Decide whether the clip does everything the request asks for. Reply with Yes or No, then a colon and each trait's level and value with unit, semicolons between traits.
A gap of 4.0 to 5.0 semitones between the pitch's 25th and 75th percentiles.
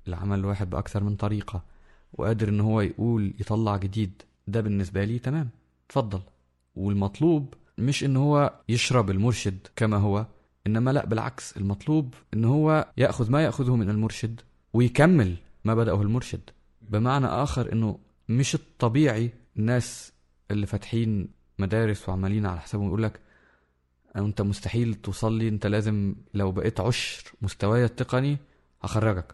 No: average, 3.4 semitones